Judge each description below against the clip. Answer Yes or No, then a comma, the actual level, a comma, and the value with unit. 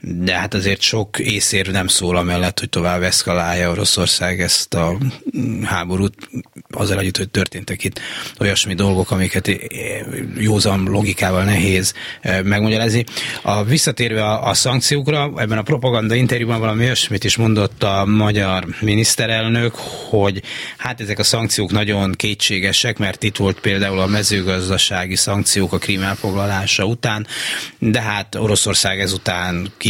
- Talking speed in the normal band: Yes, average, 130 wpm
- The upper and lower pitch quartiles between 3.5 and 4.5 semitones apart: No, average, 2.7 semitones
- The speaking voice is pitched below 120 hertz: Yes, low, 100 Hz